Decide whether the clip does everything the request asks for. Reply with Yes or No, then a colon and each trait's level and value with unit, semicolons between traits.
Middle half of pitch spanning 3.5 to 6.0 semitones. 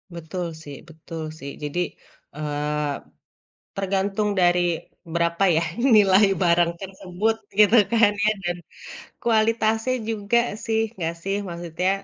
Yes: average, 3.9 semitones